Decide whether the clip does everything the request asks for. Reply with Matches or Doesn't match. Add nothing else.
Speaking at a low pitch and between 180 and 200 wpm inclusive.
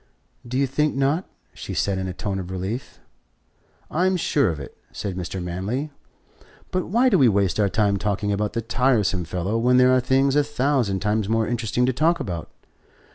Matches